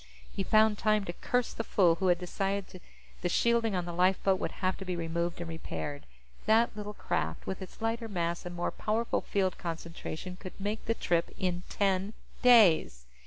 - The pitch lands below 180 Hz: No, medium, 185 Hz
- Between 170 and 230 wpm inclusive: Yes, average, 185 wpm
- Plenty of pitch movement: No, average, 3.6 semitones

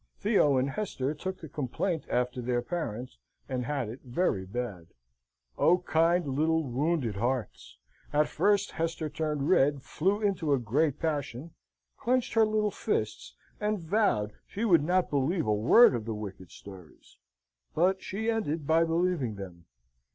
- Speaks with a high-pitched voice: No, medium, 150 Hz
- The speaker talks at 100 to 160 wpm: Yes, average, 150 wpm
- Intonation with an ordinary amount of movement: No, wide, 6.7 semitones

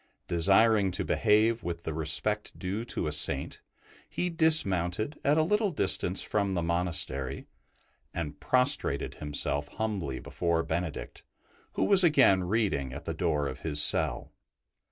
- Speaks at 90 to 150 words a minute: Yes, average, 140 wpm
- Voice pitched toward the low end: Yes, very low, 90 Hz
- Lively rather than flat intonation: Yes, wide, 6.2 semitones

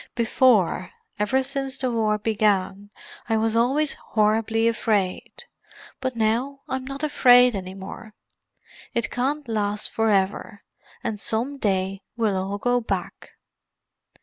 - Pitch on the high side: Yes, high, 225 Hz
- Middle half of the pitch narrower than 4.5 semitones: Yes, average, 3.6 semitones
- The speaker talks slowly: Yes, slow, 120 wpm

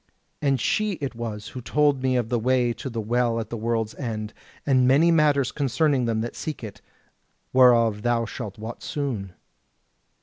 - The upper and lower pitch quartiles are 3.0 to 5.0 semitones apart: Yes, average, 3.4 semitones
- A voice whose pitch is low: Yes, low, 120 Hz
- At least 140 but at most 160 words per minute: No, average, 175 wpm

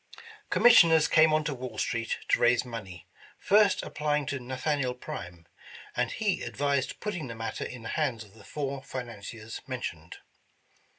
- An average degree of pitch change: Yes, average, 4.9 semitones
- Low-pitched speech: Yes, low, 130 Hz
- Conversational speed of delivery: Yes, average, 165 wpm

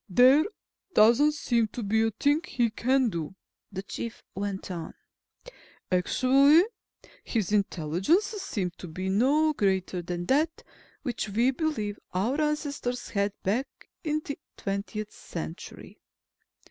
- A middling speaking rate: No, slow, 125 wpm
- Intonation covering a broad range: Yes, wide, 6.6 semitones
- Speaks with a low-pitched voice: No, high, 225 Hz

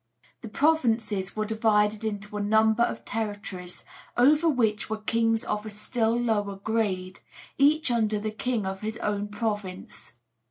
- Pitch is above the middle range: Yes, high, 215 Hz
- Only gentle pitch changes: Yes, narrow, 1.8 semitones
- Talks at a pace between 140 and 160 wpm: Yes, average, 150 wpm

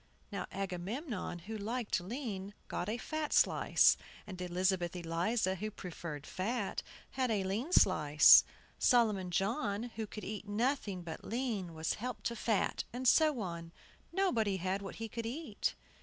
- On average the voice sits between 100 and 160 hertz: No, high, 205 Hz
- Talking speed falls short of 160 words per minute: Yes, average, 150 wpm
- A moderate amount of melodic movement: Yes, average, 4.4 semitones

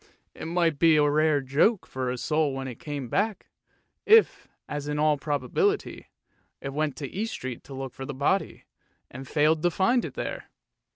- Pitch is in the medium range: Yes, medium, 150 Hz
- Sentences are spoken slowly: No, average, 185 wpm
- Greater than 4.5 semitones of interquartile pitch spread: No, average, 3.7 semitones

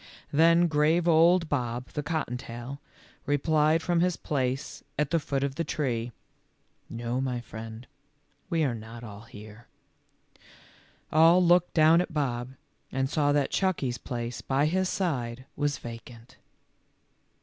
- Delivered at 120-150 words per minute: Yes, average, 140 wpm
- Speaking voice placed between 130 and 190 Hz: Yes, medium, 140 Hz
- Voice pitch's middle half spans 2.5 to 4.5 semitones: No, average, 5.2 semitones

